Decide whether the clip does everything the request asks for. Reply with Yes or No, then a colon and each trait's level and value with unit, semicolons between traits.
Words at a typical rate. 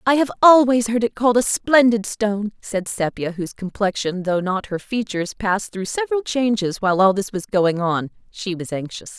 Yes: average, 195 wpm